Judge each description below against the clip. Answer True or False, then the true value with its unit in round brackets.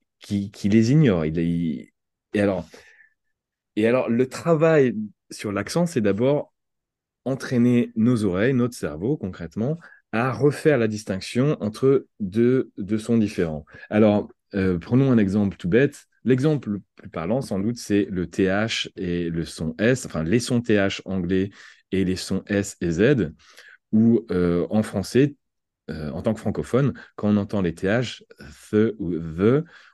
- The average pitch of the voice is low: True (105 Hz)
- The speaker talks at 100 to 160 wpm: True (155 wpm)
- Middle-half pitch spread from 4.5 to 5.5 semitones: True (5.0 semitones)